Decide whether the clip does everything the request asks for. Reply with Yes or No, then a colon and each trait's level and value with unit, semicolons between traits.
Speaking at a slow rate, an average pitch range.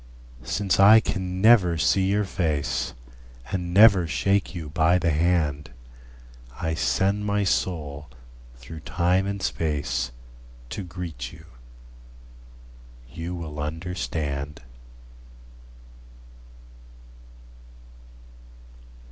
Yes: slow, 90 wpm; average, 4.2 semitones